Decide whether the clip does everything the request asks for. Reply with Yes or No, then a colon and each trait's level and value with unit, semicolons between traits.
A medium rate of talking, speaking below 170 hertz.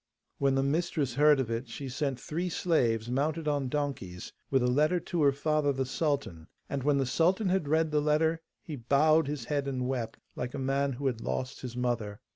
No: fast, 210 wpm; medium, 140 Hz